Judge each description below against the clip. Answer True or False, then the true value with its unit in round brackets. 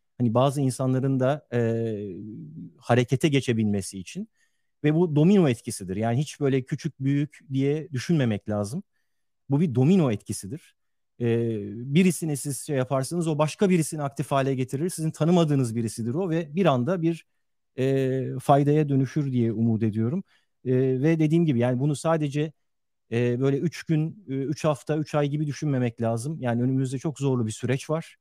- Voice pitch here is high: False (135 Hz)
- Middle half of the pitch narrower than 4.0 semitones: False (4.3 semitones)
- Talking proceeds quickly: True (155 wpm)